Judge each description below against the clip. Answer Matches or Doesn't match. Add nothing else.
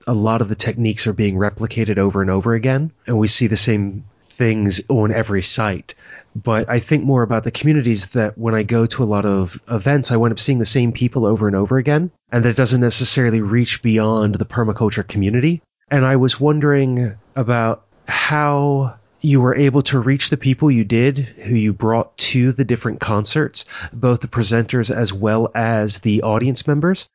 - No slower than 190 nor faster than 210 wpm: Matches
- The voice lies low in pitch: Matches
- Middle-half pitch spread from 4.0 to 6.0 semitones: Doesn't match